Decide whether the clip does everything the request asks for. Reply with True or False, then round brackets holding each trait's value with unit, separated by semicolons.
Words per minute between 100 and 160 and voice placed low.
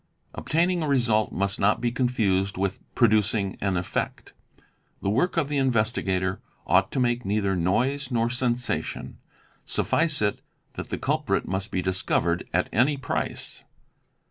True (145 wpm; 110 Hz)